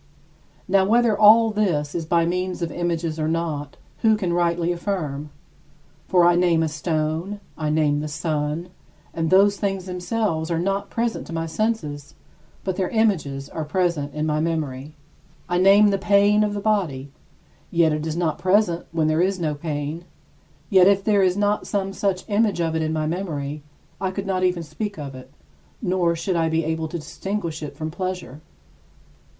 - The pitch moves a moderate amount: Yes, average, 3.9 semitones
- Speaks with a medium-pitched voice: Yes, medium, 170 Hz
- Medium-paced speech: Yes, average, 180 wpm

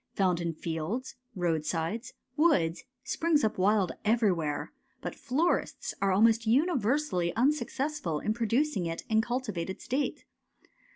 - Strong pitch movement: Yes, wide, 7.0 semitones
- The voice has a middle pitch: No, high, 220 Hz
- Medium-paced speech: No, slow, 120 wpm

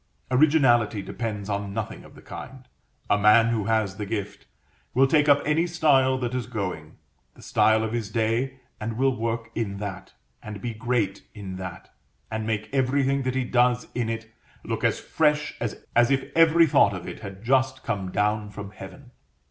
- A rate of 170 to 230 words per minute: Yes, average, 180 wpm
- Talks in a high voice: No, low, 115 Hz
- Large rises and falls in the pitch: No, average, 4.1 semitones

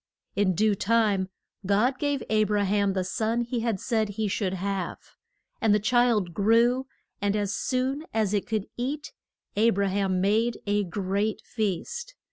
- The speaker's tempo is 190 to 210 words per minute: No, average, 165 wpm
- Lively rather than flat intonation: No, average, 2.8 semitones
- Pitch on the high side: Yes, high, 210 Hz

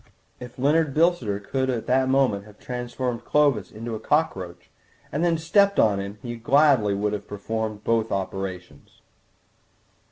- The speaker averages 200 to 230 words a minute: No, average, 155 wpm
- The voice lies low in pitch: Yes, low, 120 Hz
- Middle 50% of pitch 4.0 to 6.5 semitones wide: Yes, average, 5.1 semitones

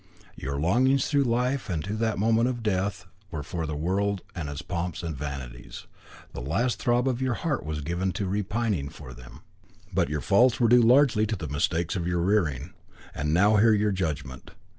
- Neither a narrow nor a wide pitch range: No, wide, 7.0 semitones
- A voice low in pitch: Yes, very low, 95 Hz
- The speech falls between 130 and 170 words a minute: No, average, 195 wpm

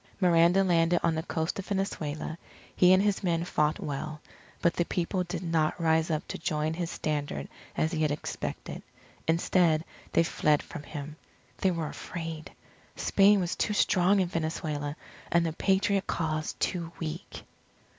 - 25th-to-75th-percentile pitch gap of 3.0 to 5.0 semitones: No, narrow, 2.5 semitones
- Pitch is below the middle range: No, medium, 165 Hz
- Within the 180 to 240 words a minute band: No, average, 160 wpm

